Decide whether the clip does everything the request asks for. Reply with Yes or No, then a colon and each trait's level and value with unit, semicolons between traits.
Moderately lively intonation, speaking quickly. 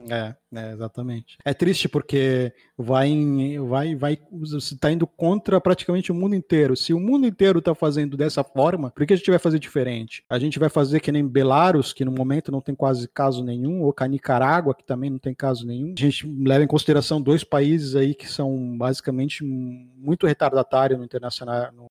Yes: average, 3.0 semitones; fast, 195 wpm